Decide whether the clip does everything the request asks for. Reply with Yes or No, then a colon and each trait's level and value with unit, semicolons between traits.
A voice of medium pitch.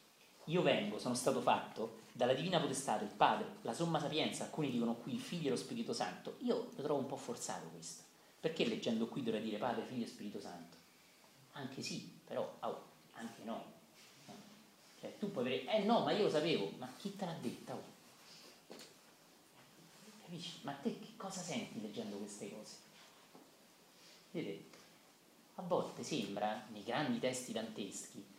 Yes: medium, 155 Hz